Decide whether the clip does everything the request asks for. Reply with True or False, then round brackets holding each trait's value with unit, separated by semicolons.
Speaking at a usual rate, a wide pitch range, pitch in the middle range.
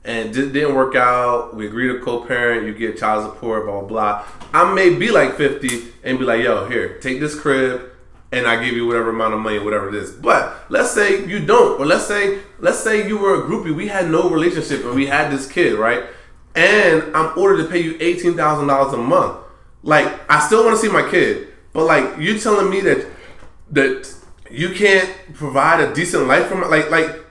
False (215 wpm; 7.9 semitones; 150 Hz)